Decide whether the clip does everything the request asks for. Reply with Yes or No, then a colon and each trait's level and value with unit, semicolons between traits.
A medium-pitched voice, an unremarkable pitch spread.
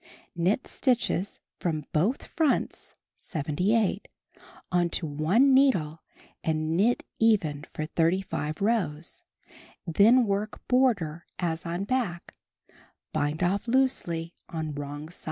No: medium, 175 Hz; wide, 6.1 semitones